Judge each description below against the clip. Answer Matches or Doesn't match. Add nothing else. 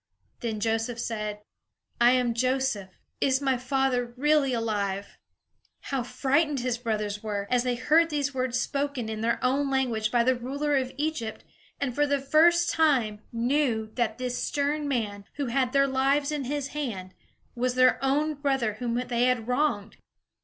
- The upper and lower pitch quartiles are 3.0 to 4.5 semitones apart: Matches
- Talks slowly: Doesn't match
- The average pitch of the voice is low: Doesn't match